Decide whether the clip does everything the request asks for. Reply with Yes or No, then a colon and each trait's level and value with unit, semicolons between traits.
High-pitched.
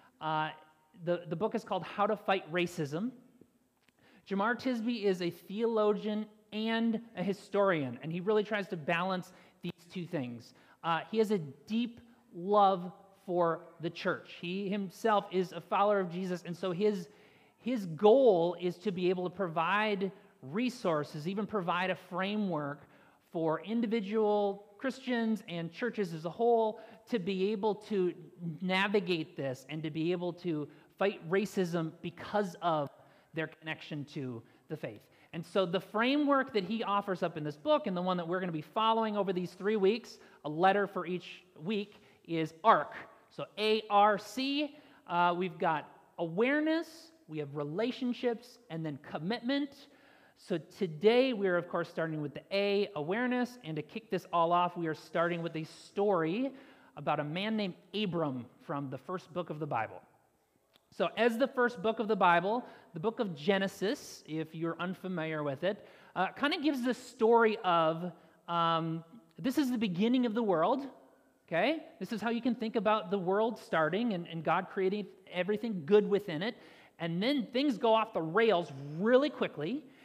Yes: high, 195 Hz